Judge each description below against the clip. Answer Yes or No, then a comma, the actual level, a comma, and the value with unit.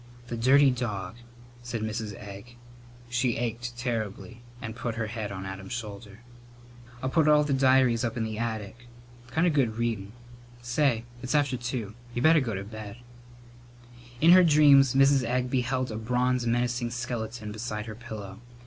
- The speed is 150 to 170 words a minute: Yes, average, 165 wpm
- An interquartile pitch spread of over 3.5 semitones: No, average, 2.7 semitones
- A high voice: No, low, 120 Hz